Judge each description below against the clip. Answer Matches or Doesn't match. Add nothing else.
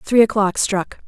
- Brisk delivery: Doesn't match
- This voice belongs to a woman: Matches